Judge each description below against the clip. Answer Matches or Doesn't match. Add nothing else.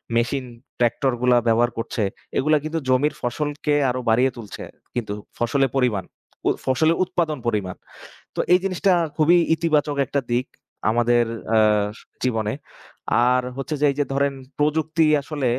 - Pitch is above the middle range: Doesn't match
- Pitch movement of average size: Matches